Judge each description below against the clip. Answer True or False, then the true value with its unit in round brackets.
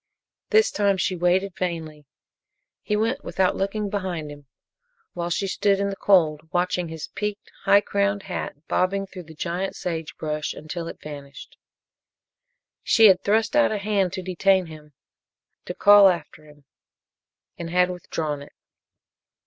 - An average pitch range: True (3.7 semitones)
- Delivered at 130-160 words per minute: True (150 wpm)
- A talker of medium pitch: True (180 Hz)